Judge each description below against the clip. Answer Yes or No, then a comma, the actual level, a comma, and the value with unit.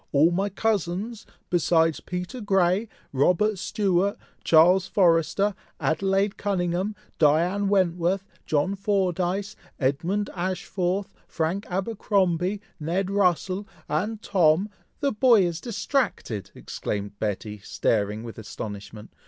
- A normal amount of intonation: Yes, average, 3.7 semitones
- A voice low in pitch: No, medium, 185 Hz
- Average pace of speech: No, slow, 105 wpm